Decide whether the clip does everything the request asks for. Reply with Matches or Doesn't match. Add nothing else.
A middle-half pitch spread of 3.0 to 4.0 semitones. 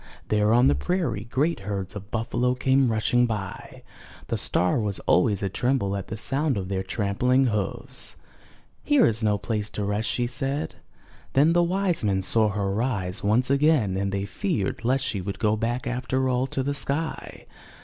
Doesn't match